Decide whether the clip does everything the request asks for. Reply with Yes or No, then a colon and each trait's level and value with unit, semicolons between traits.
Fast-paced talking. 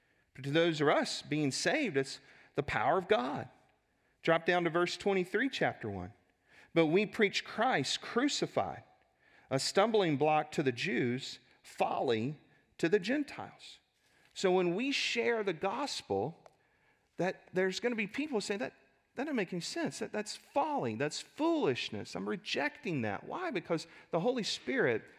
No: average, 155 wpm